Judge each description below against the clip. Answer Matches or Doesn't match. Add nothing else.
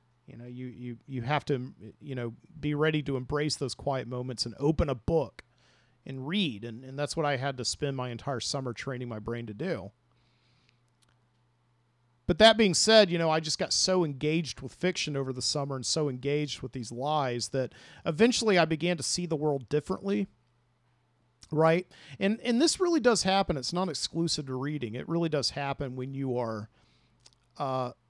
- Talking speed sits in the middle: Matches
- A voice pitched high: Doesn't match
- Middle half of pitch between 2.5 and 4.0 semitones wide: Doesn't match